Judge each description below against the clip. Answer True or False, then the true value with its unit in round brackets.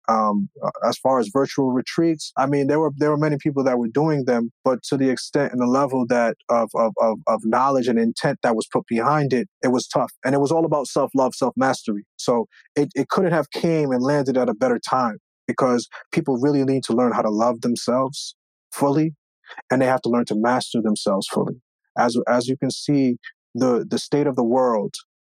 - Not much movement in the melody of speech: False (3.3 semitones)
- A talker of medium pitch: False (130 Hz)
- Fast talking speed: True (215 wpm)